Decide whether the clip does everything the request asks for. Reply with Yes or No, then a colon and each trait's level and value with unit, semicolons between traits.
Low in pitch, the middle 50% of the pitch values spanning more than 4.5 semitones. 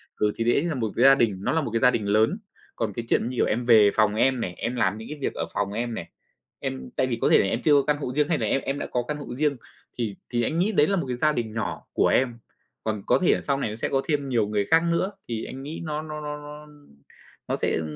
Yes: low, 125 Hz; average, 5.0 semitones